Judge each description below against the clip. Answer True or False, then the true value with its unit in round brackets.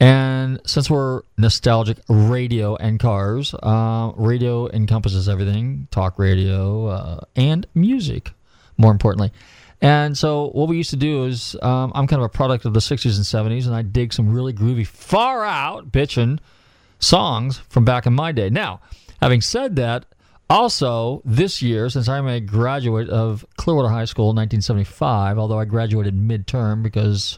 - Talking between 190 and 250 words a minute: False (160 wpm)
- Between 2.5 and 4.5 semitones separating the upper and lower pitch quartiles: True (3.4 semitones)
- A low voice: True (115 Hz)